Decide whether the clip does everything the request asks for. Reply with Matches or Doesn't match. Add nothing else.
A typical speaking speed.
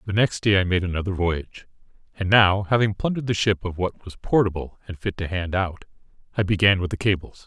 Doesn't match